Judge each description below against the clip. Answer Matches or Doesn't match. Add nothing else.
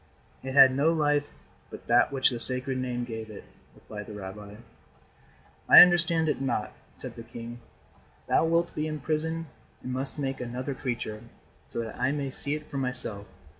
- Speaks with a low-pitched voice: Matches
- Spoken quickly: Doesn't match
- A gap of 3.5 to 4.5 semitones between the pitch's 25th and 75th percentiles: Matches